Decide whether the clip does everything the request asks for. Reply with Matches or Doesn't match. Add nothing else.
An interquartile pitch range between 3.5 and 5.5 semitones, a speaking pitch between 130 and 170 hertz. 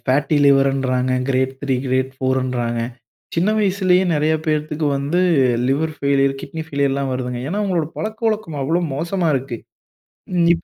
Matches